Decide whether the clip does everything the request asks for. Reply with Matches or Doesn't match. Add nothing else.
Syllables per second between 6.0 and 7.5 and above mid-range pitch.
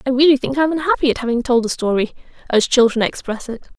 Matches